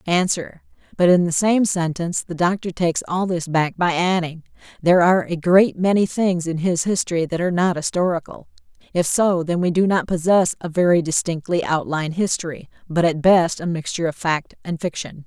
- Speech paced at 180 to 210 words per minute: Yes, average, 190 wpm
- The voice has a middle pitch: Yes, medium, 170 Hz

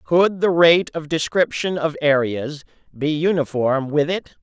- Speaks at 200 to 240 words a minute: No, average, 150 wpm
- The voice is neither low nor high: Yes, medium, 155 Hz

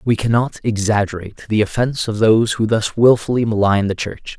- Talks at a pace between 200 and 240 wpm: No, average, 180 wpm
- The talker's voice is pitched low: Yes, low, 110 Hz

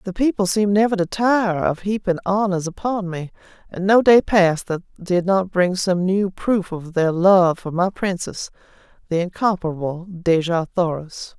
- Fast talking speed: No, average, 170 wpm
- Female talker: Yes, female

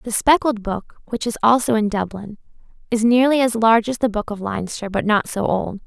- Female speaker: Yes, female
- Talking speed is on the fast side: Yes, fast, 215 wpm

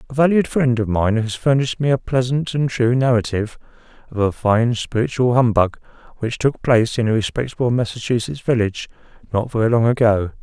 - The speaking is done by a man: Yes, male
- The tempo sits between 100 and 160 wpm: No, average, 175 wpm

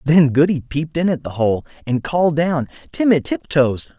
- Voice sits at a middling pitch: Yes, medium, 150 Hz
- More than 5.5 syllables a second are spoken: No, 5.0 syllables/s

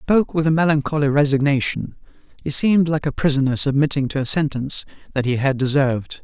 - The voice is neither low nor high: Yes, medium, 145 Hz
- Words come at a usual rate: Yes, average, 175 wpm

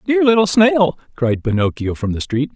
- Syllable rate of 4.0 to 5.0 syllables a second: Yes, 4.9 syllables/s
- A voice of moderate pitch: Yes, medium, 165 Hz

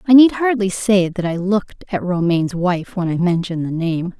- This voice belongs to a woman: Yes, female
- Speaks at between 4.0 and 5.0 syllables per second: No, 5.4 syllables/s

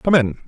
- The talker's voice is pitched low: No, medium, 145 Hz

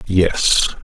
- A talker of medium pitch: No, very low, 90 Hz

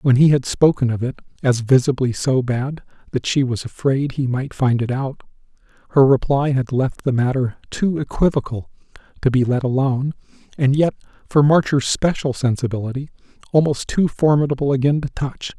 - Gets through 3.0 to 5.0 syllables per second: No, 5.2 syllables/s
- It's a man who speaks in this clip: Yes, male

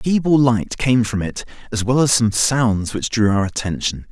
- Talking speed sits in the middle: No, fast, 220 wpm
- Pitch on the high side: No, low, 115 Hz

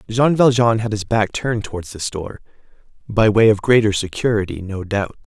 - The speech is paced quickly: No, average, 180 wpm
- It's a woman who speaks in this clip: No, male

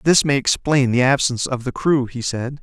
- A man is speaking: Yes, male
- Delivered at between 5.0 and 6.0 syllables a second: Yes, 5.2 syllables/s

